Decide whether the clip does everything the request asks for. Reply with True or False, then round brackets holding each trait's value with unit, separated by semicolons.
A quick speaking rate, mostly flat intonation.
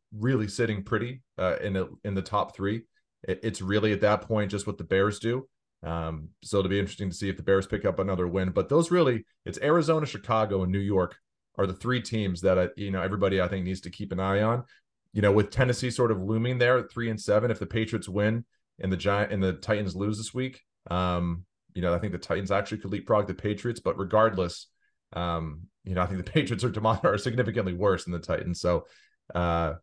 False (235 wpm; 3.2 semitones)